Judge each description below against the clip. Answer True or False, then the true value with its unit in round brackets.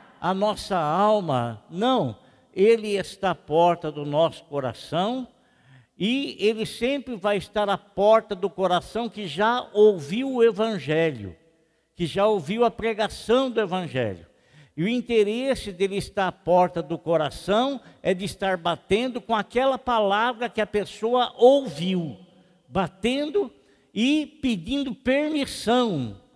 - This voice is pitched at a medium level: False (205 Hz)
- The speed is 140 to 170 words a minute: False (125 wpm)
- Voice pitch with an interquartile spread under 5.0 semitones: False (5.4 semitones)